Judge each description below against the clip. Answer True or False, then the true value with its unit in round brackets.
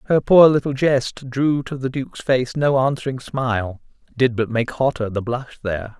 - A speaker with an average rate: True (190 wpm)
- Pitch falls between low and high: False (130 Hz)